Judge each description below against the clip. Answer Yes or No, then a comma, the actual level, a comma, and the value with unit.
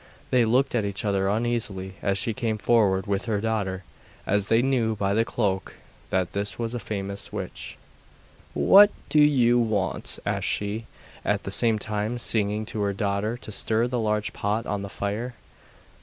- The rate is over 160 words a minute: Yes, average, 175 wpm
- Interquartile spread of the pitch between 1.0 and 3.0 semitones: Yes, average, 2.7 semitones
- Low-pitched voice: Yes, low, 110 Hz